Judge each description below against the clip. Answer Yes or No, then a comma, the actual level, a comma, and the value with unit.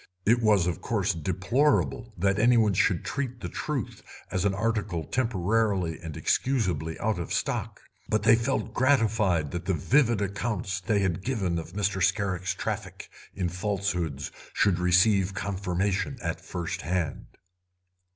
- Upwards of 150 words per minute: No, average, 145 wpm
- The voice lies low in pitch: Yes, very low, 95 Hz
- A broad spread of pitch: No, average, 3.8 semitones